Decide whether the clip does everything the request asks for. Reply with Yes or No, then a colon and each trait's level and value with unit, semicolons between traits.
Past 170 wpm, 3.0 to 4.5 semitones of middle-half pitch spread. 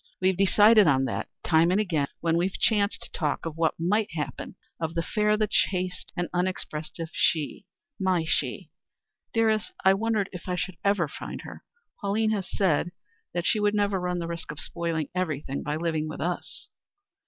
Yes: average, 185 wpm; average, 3.8 semitones